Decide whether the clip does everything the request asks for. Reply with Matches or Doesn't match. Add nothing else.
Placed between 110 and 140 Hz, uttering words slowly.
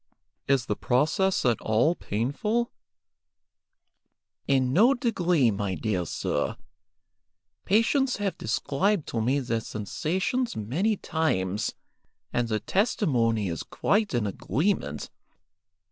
Matches